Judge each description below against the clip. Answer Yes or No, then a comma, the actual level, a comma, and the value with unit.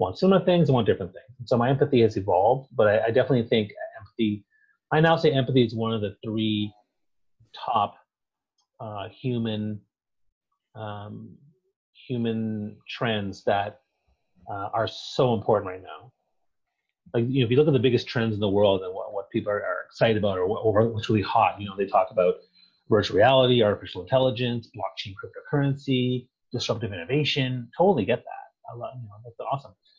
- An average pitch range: Yes, average, 3.9 semitones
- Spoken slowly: No, average, 180 wpm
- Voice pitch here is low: Yes, low, 120 Hz